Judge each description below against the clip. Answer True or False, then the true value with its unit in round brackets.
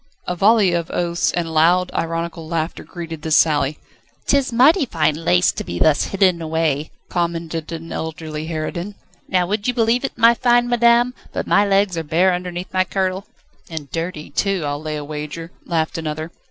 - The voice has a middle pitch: True (170 Hz)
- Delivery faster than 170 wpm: True (180 wpm)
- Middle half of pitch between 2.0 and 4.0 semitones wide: True (3.7 semitones)